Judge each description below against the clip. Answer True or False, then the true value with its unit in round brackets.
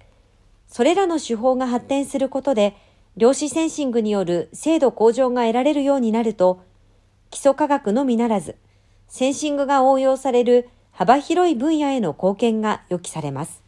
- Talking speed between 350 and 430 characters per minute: False (330 characters per minute)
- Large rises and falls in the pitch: True (7.0 semitones)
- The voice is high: True (240 Hz)